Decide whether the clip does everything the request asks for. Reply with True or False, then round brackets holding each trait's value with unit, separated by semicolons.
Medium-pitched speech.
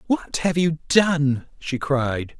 True (150 Hz)